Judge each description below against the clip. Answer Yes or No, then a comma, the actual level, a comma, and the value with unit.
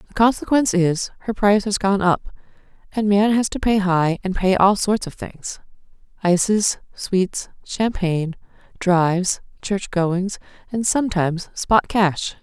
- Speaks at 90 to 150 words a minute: Yes, average, 140 wpm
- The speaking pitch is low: No, high, 195 Hz